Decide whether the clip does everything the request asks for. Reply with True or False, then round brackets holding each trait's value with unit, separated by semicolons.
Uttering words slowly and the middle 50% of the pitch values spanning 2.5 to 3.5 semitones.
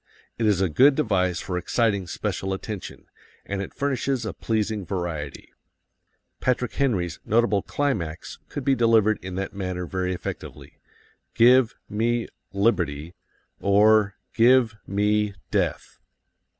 False (125 wpm; 4.1 semitones)